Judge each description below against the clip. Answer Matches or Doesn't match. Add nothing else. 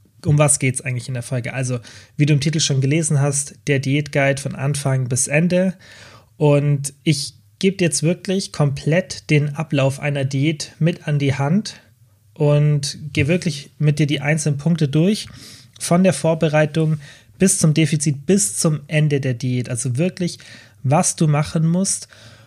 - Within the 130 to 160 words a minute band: Doesn't match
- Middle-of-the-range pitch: Matches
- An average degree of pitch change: Matches